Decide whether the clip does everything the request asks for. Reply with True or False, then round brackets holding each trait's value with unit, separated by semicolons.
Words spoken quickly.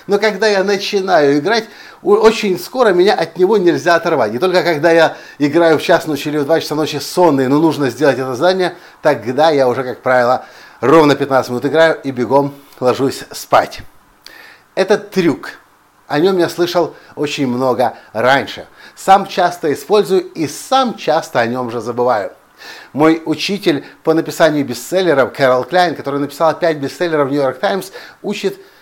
True (165 wpm)